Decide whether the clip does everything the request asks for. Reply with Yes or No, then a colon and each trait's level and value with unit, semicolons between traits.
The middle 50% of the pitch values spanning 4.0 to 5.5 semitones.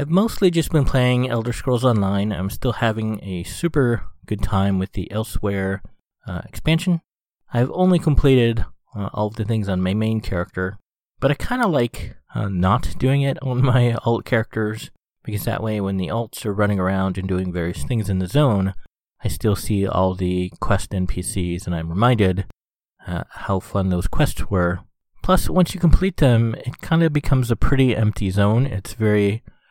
Yes: average, 4.7 semitones